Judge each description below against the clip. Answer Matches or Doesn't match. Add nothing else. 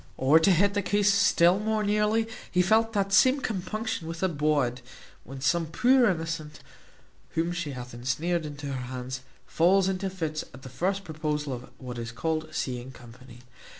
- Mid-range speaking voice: Matches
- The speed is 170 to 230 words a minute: Matches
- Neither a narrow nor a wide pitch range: Doesn't match